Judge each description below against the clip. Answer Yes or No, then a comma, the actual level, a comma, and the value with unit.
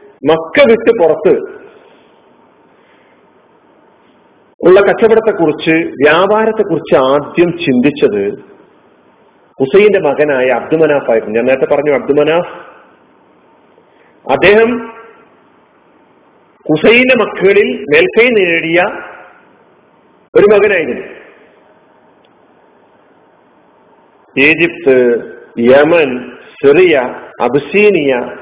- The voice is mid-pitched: No, high, 200 Hz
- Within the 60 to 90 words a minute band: Yes, average, 65 wpm